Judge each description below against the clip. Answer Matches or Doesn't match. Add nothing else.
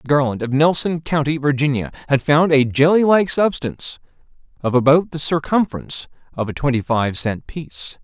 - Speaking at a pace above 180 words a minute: Doesn't match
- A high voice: Doesn't match